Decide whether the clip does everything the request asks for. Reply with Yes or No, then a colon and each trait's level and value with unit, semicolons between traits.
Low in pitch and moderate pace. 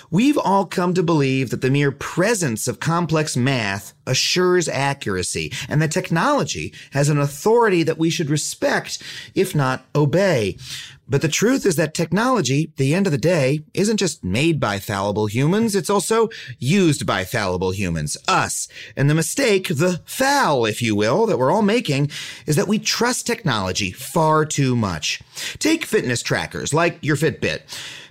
No: medium, 155 Hz; average, 165 wpm